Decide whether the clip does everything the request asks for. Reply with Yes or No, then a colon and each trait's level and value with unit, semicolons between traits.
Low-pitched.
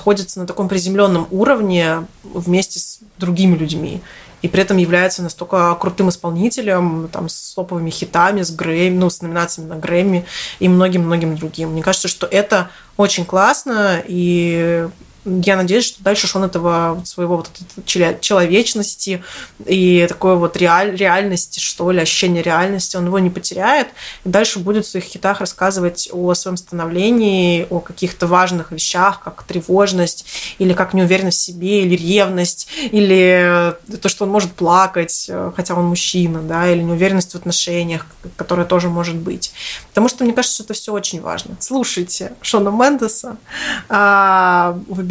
No: medium, 180 Hz